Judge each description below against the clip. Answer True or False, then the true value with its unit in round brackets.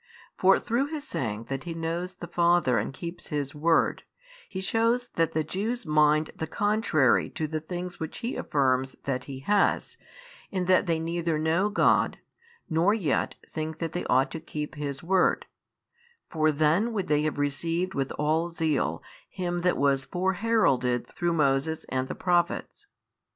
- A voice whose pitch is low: False (165 Hz)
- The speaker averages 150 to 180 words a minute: True (165 wpm)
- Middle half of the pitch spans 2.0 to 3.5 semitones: False (4.0 semitones)